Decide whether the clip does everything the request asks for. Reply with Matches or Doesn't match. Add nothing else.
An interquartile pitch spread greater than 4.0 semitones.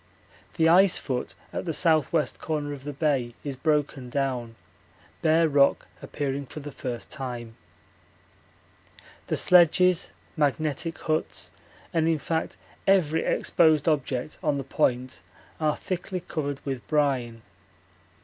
Doesn't match